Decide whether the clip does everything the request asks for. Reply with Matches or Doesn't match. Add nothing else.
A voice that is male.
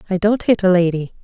Doesn't match